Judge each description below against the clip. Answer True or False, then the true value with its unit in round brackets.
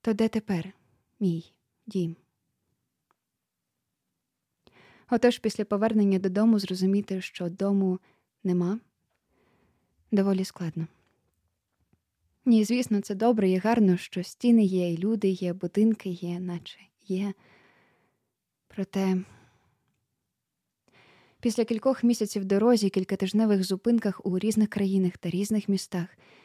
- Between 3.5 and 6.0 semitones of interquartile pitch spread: False (2.9 semitones)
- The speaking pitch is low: False (195 Hz)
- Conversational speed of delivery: False (100 wpm)